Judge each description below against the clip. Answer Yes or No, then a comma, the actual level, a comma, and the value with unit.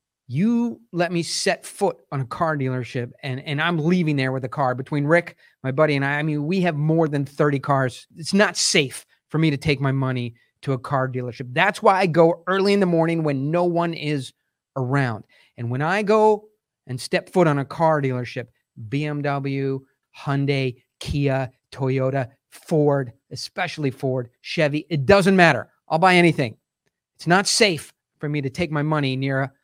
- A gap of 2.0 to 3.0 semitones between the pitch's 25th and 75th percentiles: No, average, 4.3 semitones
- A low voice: No, medium, 145 Hz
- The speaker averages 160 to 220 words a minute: Yes, average, 190 wpm